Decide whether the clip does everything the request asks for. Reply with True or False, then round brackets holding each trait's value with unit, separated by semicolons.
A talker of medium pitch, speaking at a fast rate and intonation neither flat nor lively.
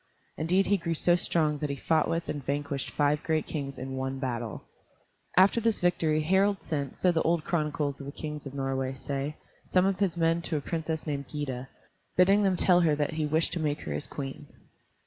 True (155 Hz; 210 wpm; 3.3 semitones)